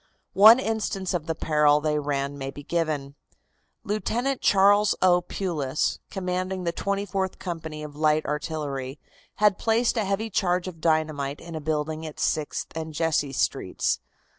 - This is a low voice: No, medium, 160 Hz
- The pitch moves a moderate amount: Yes, average, 4.3 semitones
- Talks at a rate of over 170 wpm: No, average, 155 wpm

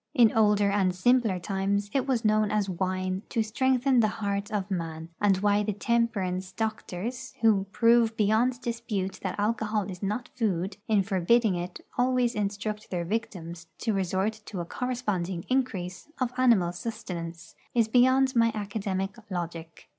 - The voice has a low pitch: No, high, 205 Hz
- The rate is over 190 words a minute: No, average, 155 wpm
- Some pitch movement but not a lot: Yes, average, 3.7 semitones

